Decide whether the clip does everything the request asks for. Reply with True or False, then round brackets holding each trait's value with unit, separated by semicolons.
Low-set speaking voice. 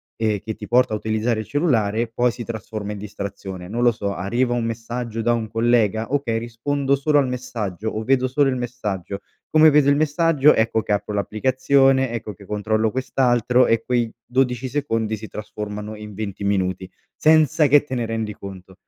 True (115 Hz)